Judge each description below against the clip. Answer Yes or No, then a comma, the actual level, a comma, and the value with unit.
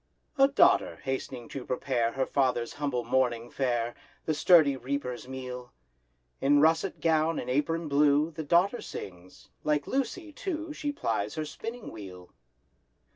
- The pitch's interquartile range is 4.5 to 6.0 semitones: Yes, average, 4.9 semitones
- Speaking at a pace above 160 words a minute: No, average, 140 wpm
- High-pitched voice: No, medium, 140 Hz